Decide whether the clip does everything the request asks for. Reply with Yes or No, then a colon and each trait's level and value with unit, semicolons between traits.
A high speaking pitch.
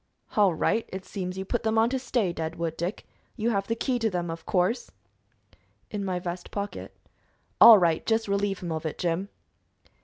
Yes: high, 195 Hz